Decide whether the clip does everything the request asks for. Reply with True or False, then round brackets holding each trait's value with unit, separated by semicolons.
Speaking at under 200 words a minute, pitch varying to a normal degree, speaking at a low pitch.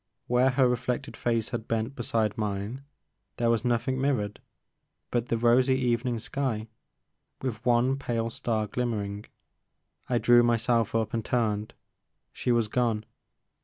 False (140 wpm; 2.0 semitones; 120 Hz)